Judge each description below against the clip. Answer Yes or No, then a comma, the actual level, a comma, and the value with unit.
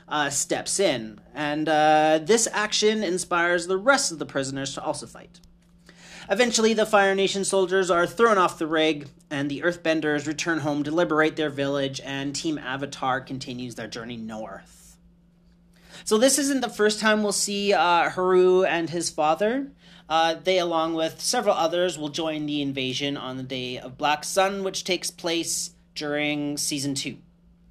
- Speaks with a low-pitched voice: No, medium, 165 Hz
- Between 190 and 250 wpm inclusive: No, average, 165 wpm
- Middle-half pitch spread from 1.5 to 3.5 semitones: No, average, 3.9 semitones